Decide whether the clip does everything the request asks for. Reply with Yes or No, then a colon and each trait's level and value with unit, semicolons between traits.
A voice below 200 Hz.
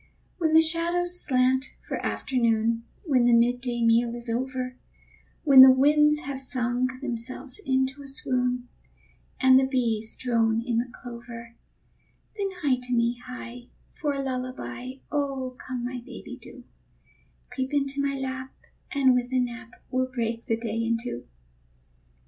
No: very high, 255 Hz